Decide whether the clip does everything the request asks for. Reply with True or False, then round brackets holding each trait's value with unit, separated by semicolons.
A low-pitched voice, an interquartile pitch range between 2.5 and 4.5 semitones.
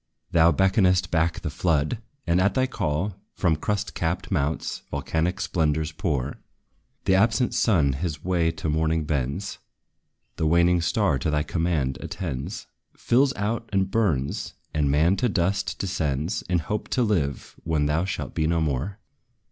True (85 Hz; 4.0 semitones)